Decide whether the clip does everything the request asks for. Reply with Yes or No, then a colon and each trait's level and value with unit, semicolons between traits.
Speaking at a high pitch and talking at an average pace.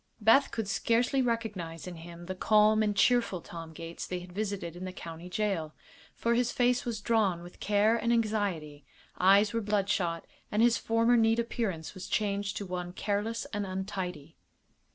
Yes: high, 205 Hz; average, 175 wpm